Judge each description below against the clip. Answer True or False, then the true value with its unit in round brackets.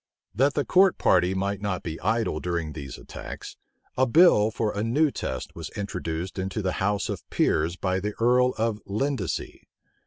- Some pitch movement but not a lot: True (4.2 semitones)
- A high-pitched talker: False (100 Hz)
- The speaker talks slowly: False (175 wpm)